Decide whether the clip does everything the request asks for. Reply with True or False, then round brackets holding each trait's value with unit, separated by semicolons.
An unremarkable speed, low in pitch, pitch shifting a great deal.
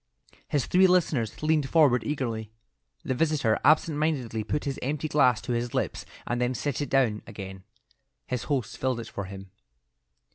False (170 wpm; 130 Hz; 4.8 semitones)